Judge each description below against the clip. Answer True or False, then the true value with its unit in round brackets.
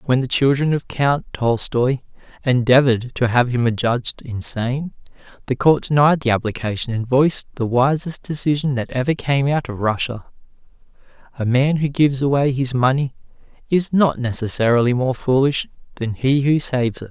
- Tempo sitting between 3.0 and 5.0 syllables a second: False (5.3 syllables/s)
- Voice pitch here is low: True (130 Hz)